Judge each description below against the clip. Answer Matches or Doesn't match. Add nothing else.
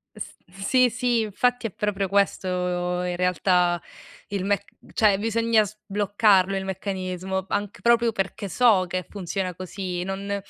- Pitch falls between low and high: Doesn't match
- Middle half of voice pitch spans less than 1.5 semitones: Doesn't match